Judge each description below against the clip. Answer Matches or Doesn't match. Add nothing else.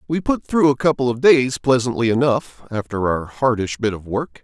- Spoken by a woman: Doesn't match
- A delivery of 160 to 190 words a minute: Doesn't match